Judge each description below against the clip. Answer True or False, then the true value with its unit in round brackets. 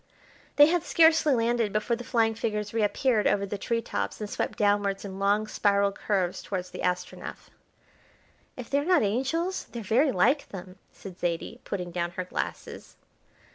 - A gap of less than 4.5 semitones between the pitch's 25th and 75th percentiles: True (3.8 semitones)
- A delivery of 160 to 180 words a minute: True (165 wpm)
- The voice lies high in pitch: True (210 Hz)